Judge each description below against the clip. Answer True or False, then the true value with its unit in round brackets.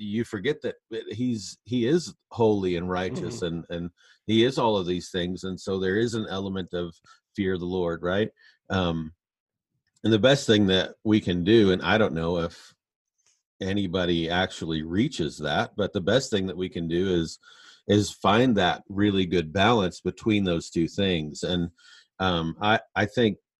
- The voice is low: True (95 Hz)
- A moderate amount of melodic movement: True (3.5 semitones)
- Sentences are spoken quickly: False (180 wpm)